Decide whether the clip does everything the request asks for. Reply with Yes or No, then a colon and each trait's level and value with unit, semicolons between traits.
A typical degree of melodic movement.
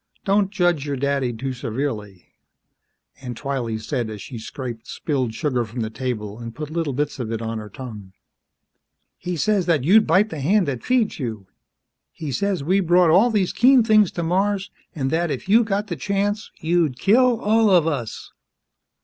No: wide, 8.1 semitones